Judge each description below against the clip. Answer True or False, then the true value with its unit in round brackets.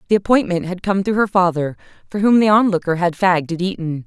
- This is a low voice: False (185 Hz)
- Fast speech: True (220 wpm)